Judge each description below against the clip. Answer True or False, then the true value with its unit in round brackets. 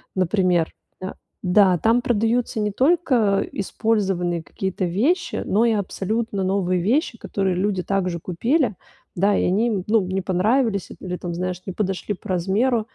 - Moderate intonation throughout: True (3.6 semitones)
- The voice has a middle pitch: False (195 Hz)